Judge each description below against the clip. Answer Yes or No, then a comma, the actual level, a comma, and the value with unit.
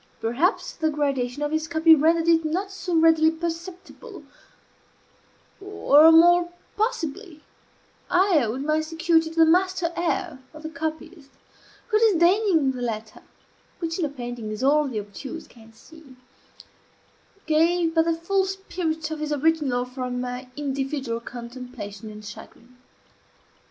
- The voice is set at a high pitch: Yes, very high, 315 Hz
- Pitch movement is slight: No, average, 4.5 semitones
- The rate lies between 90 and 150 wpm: Yes, slow, 135 wpm